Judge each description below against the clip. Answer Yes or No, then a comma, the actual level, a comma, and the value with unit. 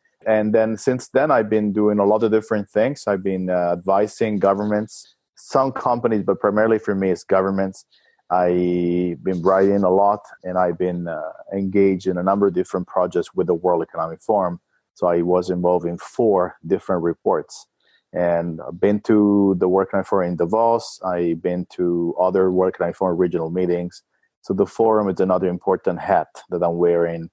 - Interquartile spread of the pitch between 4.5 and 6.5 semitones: No, narrow, 2.6 semitones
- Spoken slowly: No, average, 180 wpm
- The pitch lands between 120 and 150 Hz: No, very low, 95 Hz